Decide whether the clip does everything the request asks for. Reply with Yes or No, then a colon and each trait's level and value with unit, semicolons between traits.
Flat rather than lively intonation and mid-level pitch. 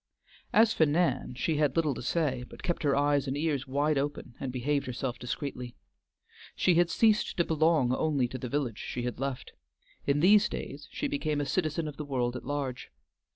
No: average, 3.5 semitones; medium, 145 Hz